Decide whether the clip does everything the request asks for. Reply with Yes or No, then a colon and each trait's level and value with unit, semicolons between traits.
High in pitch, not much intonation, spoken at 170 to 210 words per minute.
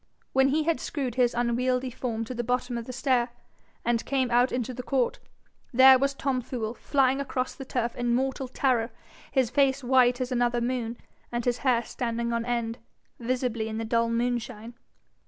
Yes: high, 245 Hz; narrow, 1.7 semitones; average, 185 wpm